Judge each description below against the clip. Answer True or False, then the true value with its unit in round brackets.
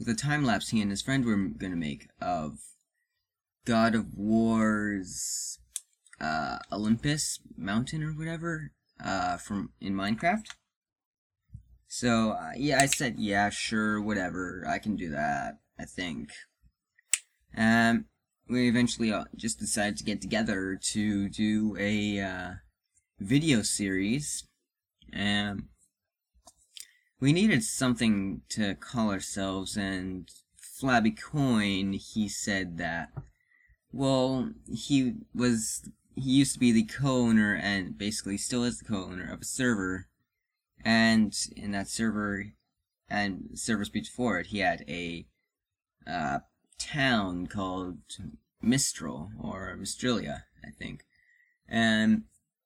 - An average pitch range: True (3.7 semitones)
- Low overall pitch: True (110 Hz)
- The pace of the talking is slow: True (120 wpm)